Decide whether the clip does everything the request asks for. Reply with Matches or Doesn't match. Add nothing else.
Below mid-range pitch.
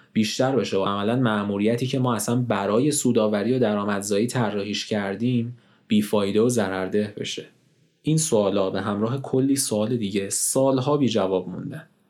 Matches